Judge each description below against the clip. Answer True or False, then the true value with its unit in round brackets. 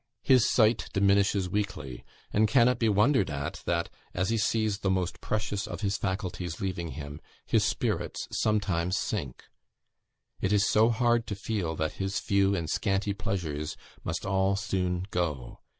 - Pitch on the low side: True (100 Hz)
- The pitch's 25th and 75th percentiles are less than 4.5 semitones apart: True (3.2 semitones)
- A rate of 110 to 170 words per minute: True (160 wpm)